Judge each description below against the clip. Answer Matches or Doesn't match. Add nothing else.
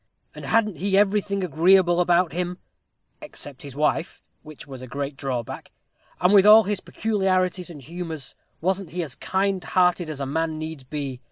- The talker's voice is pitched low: Doesn't match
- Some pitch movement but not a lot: Matches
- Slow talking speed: Doesn't match